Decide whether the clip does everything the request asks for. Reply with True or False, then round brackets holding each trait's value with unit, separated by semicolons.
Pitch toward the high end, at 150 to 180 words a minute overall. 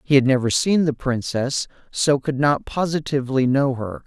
False (135 Hz; 175 wpm)